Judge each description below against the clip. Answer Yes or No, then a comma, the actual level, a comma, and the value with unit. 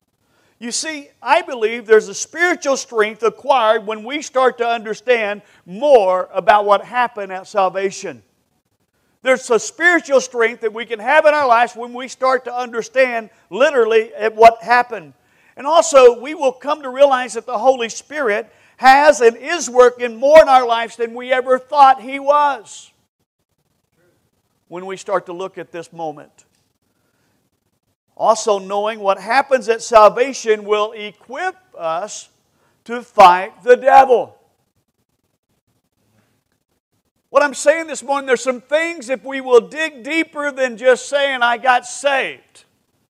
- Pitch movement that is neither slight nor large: Yes, average, 4.5 semitones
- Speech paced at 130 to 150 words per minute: Yes, average, 145 wpm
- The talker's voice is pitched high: Yes, high, 240 Hz